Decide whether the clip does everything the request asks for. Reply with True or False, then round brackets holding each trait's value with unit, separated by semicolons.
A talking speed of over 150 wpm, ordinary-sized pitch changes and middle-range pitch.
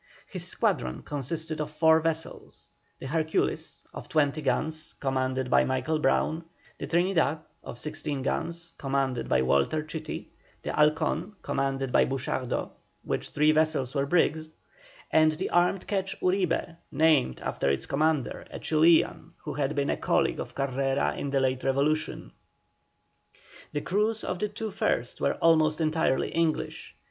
False (145 wpm; 3.1 semitones; 155 Hz)